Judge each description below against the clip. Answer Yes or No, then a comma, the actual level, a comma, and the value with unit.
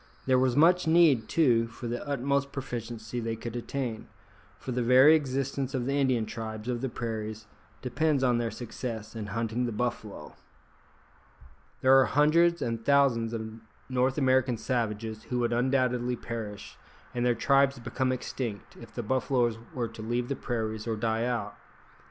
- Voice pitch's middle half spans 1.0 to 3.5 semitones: Yes, average, 2.7 semitones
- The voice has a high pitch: No, low, 120 Hz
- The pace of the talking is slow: No, average, 165 wpm